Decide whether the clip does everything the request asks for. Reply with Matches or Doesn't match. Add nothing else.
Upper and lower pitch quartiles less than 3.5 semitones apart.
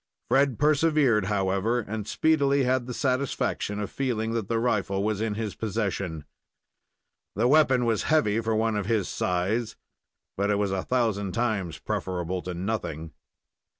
Doesn't match